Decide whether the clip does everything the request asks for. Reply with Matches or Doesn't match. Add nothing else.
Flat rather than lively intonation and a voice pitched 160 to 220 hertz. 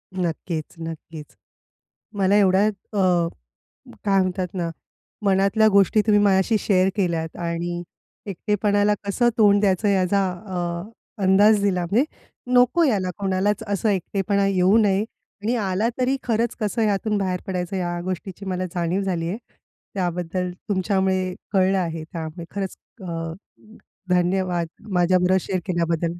Matches